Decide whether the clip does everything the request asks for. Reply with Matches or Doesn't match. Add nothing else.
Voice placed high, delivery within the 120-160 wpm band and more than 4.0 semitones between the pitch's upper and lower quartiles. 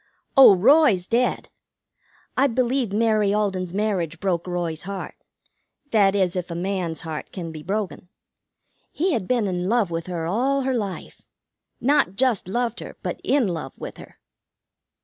Matches